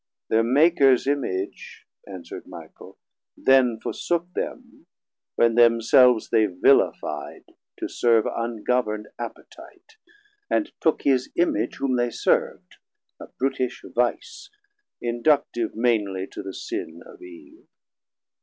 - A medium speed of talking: No, slow, 105 wpm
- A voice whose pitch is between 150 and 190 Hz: No, low, 125 Hz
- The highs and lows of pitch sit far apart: No, average, 4.1 semitones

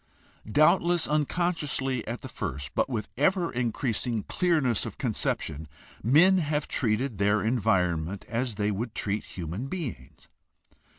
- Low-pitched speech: Yes, low, 120 Hz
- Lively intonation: Yes, wide, 6.5 semitones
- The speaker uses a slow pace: Yes, slow, 125 wpm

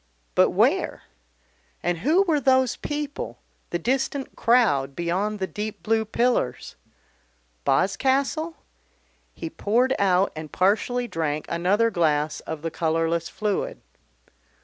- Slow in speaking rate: Yes, slow, 115 wpm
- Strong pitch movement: Yes, wide, 7.2 semitones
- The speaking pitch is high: Yes, high, 205 Hz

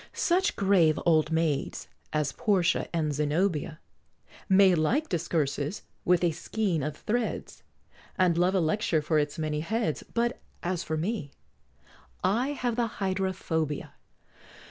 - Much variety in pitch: No, average, 4.5 semitones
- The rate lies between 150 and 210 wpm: No, slow, 135 wpm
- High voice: No, medium, 175 Hz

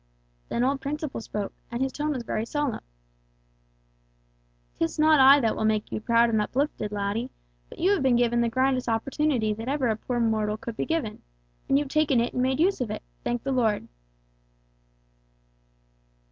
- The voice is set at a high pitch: Yes, high, 245 Hz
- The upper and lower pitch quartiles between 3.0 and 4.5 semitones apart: Yes, average, 3.8 semitones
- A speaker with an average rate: Yes, average, 180 wpm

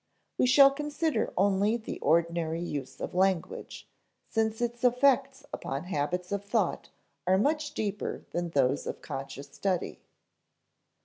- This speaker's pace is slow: Yes, slow, 130 wpm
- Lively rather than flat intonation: Yes, wide, 6.7 semitones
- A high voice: Yes, high, 200 Hz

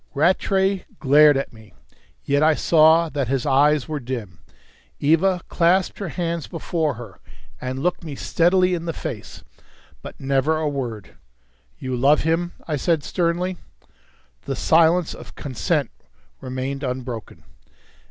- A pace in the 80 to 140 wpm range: Yes, slow, 135 wpm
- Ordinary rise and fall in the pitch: Yes, average, 4.2 semitones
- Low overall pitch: No, medium, 150 Hz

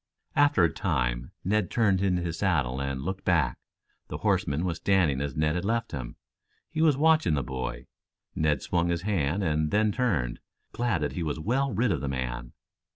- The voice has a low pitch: Yes, very low, 85 Hz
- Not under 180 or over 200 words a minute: Yes, average, 190 wpm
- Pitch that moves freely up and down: Yes, wide, 6.6 semitones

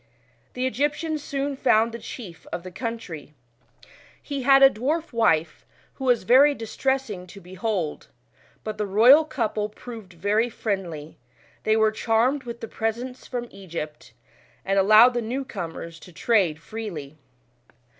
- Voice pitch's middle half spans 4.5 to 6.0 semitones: Yes, average, 5.1 semitones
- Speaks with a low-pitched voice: No, high, 220 Hz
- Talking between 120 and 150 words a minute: Yes, average, 145 wpm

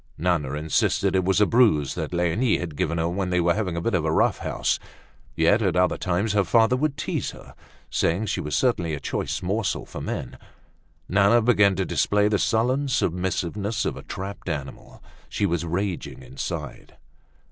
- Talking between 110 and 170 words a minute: No, average, 185 wpm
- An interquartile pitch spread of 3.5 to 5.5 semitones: Yes, average, 3.8 semitones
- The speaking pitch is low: Yes, very low, 95 Hz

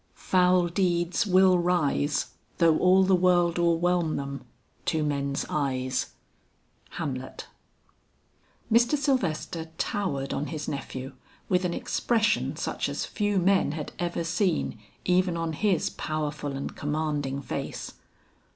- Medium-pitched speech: Yes, medium, 170 Hz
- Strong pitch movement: No, average, 3.8 semitones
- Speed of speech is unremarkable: No, slow, 120 wpm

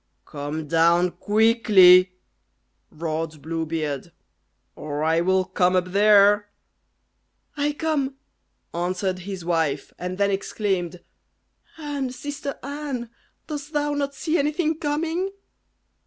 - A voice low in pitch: No, high, 195 Hz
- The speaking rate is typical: No, slow, 110 wpm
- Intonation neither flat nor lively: No, wide, 8.9 semitones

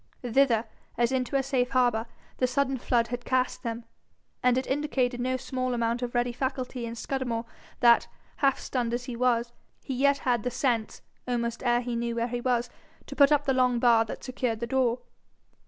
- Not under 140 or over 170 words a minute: No, average, 195 wpm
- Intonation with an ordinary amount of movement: No, narrow, 1.6 semitones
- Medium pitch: No, high, 245 Hz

